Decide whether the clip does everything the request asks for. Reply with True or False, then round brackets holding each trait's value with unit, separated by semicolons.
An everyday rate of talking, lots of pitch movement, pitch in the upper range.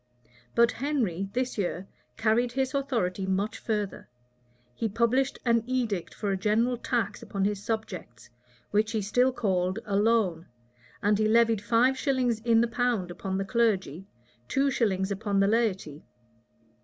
False (150 wpm; 3.6 semitones; 220 Hz)